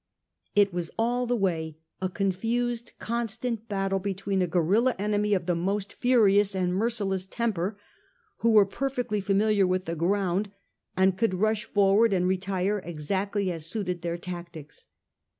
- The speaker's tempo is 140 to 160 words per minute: Yes, average, 150 wpm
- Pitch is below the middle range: No, high, 195 Hz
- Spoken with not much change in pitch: No, average, 3.0 semitones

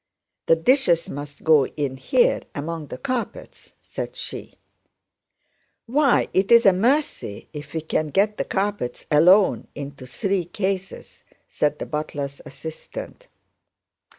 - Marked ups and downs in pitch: Yes, wide, 6.0 semitones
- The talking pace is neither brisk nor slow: No, slow, 125 wpm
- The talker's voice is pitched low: No, medium, 165 Hz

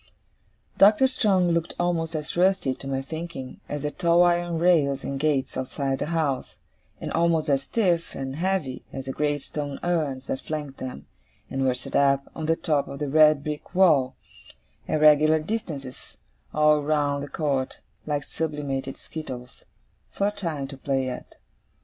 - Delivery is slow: No, average, 165 wpm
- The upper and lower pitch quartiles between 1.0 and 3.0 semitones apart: No, average, 3.6 semitones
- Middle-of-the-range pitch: Yes, medium, 150 Hz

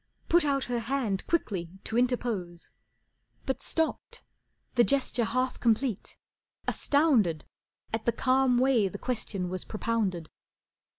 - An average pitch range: Yes, average, 4.8 semitones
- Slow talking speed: Yes, slow, 120 wpm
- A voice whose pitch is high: Yes, high, 240 Hz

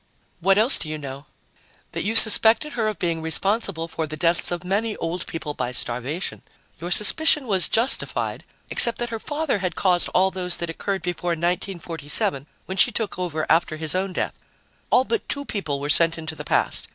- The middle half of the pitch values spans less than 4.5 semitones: No, average, 4.8 semitones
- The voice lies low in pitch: No, medium, 180 Hz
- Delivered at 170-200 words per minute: Yes, average, 190 wpm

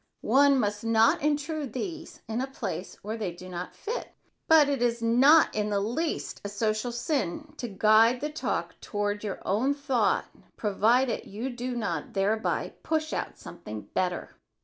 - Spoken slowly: No, average, 165 wpm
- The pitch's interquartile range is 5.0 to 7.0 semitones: Yes, average, 5.3 semitones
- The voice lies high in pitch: Yes, high, 230 Hz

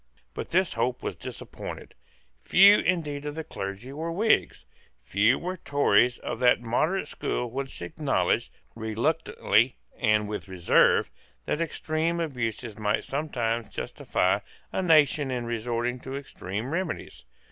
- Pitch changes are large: Yes, wide, 5.7 semitones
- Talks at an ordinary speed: No, slow, 130 wpm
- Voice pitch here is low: Yes, low, 125 Hz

